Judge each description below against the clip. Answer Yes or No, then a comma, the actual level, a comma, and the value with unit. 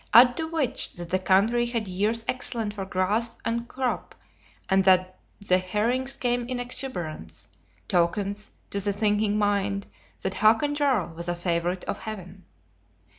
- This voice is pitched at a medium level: No, high, 205 Hz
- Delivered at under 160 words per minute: Yes, average, 150 wpm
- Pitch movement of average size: Yes, average, 4.3 semitones